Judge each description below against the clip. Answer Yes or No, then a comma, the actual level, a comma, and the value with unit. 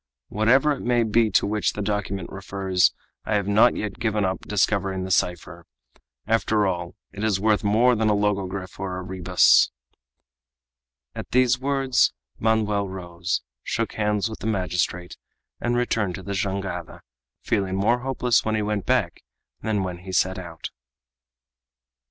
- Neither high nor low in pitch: No, low, 100 Hz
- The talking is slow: No, average, 155 wpm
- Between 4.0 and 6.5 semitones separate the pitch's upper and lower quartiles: No, average, 2.8 semitones